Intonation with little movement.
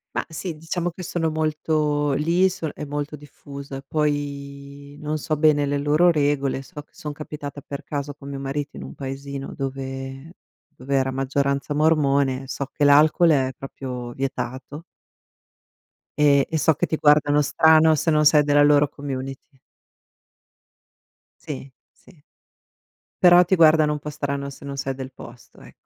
Yes: narrow, 1.8 semitones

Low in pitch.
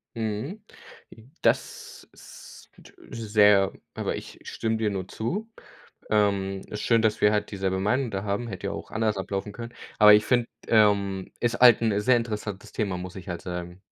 Yes: low, 105 Hz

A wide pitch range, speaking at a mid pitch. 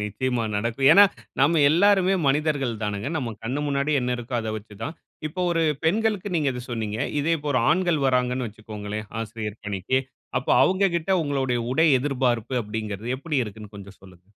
No: wide, 6.1 semitones; low, 125 Hz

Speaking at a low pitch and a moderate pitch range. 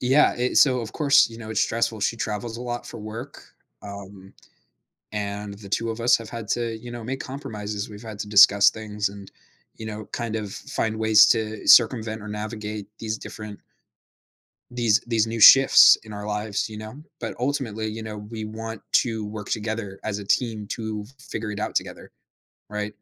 No: low, 110 Hz; narrow, 1.8 semitones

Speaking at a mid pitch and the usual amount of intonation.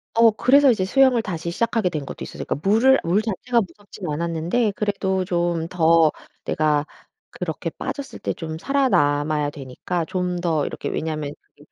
No: medium, 180 Hz; wide, 5.8 semitones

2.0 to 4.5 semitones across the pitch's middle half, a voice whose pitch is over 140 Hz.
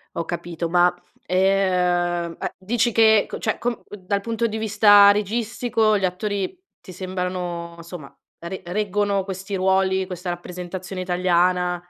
Yes: narrow, 2.5 semitones; high, 190 Hz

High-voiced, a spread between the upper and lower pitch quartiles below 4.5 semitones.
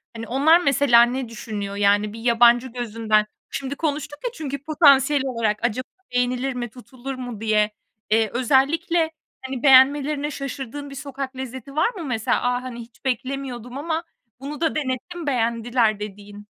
Yes: very high, 255 Hz; average, 3.4 semitones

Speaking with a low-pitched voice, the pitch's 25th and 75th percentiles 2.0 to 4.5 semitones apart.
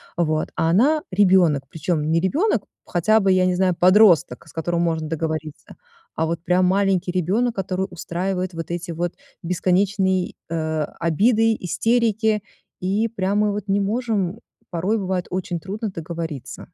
No: medium, 185 Hz; average, 3.3 semitones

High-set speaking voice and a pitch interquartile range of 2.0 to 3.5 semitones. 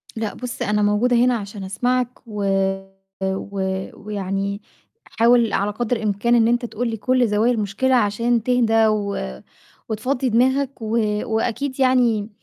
Yes: high, 225 Hz; average, 2.9 semitones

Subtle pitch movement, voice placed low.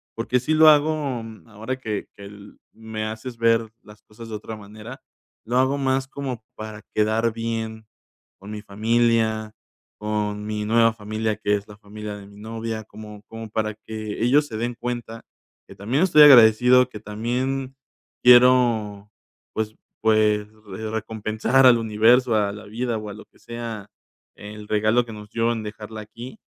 Yes: narrow, 2.0 semitones; low, 110 Hz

